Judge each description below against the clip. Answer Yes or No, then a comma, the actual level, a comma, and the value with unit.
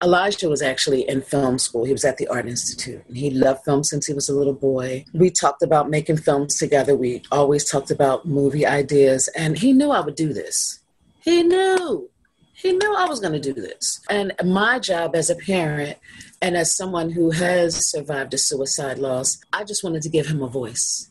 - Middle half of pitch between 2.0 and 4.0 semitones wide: No, average, 4.6 semitones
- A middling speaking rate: No, fast, 210 wpm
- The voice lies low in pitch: No, medium, 150 Hz